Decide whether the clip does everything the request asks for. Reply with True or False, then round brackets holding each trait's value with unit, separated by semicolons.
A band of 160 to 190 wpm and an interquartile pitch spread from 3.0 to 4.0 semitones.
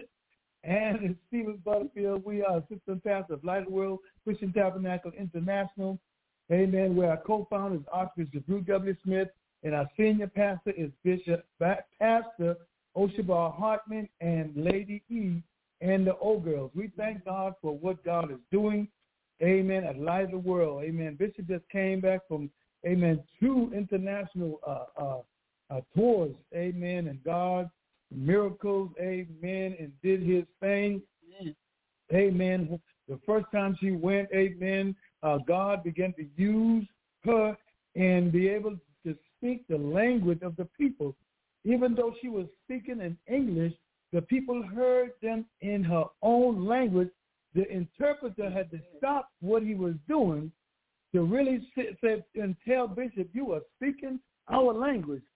False (150 wpm; 3.6 semitones)